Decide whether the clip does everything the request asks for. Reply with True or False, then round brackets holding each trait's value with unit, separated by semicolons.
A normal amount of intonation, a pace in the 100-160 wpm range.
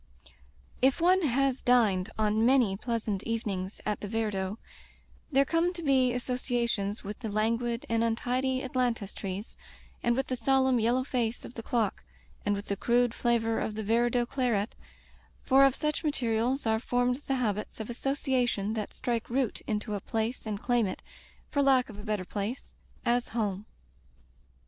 False (3.1 semitones; 180 wpm)